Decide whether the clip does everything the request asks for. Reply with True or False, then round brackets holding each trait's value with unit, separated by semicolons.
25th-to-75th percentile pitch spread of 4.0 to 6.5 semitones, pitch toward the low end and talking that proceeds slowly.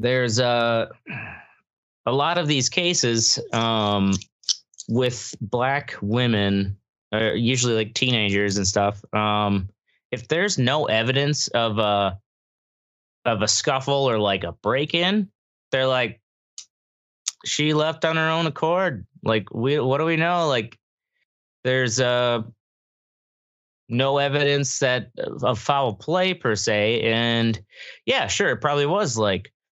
True (5.1 semitones; 120 Hz; 130 wpm)